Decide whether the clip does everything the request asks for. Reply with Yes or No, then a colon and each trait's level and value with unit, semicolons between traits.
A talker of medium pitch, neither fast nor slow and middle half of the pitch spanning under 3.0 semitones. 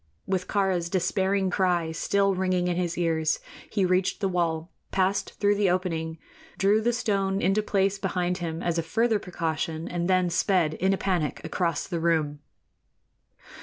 Yes: medium, 180 Hz; average, 165 wpm; narrow, 2.6 semitones